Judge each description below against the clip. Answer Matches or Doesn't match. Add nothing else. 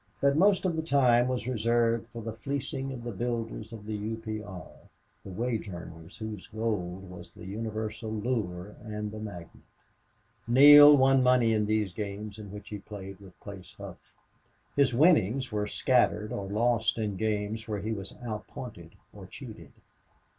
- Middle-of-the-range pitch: Doesn't match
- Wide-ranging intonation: Doesn't match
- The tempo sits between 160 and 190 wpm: Matches